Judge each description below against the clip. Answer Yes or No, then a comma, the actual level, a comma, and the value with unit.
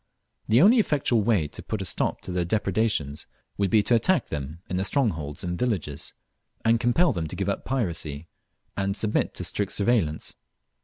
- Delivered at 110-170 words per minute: No, average, 185 wpm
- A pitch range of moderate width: No, wide, 5.8 semitones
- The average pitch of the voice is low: Yes, low, 100 Hz